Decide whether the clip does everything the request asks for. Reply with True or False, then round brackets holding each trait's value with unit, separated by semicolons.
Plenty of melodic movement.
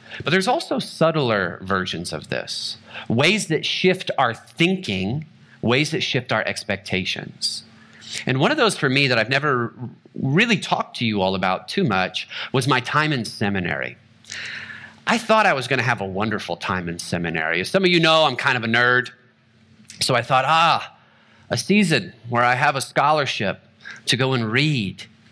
True (7.0 semitones)